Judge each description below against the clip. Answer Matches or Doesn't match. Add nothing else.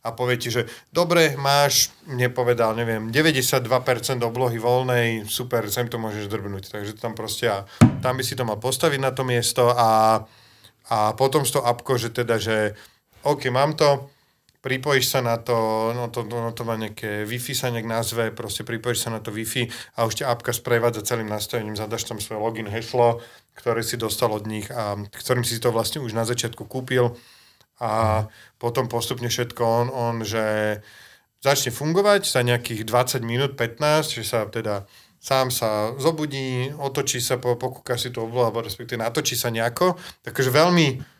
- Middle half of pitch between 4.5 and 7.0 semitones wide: Doesn't match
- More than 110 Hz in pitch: Matches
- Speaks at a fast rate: Matches